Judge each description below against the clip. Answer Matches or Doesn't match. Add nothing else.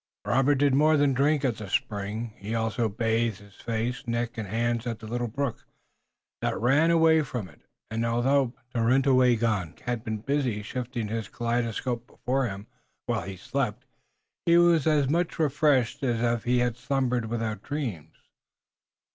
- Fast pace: Doesn't match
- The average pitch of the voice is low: Matches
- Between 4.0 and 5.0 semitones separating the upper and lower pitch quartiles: Doesn't match